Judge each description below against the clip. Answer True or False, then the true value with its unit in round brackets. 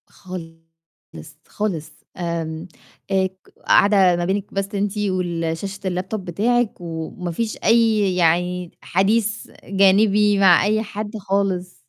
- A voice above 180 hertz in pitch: True (190 Hz)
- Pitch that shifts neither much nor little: True (3.0 semitones)